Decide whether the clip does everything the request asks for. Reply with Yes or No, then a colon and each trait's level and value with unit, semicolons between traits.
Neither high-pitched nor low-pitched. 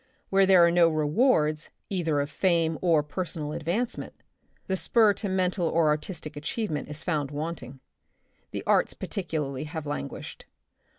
Yes: medium, 165 Hz